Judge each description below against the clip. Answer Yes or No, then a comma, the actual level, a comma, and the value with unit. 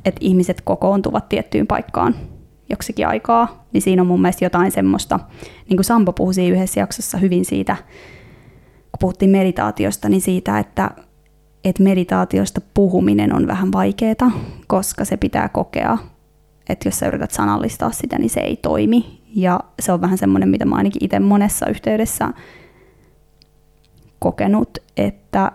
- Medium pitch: Yes, medium, 180 Hz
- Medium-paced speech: Yes, average, 145 wpm